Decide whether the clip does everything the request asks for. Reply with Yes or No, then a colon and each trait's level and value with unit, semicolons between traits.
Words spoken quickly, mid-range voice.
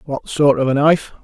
Yes: fast, 245 wpm; medium, 145 Hz